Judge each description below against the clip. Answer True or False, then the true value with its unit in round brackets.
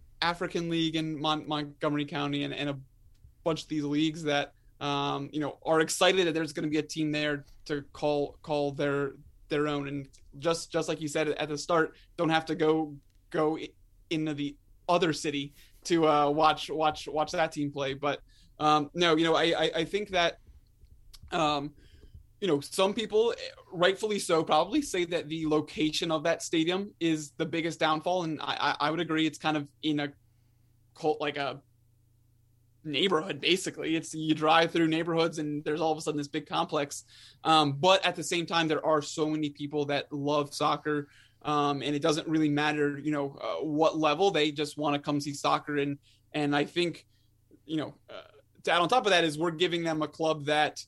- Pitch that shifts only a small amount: True (2.1 semitones)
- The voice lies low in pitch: False (155 Hz)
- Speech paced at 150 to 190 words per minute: False (200 wpm)